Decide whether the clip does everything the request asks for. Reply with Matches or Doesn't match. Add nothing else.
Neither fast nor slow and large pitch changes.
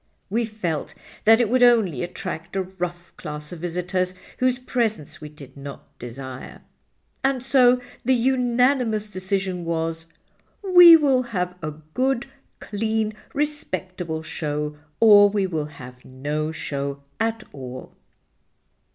Doesn't match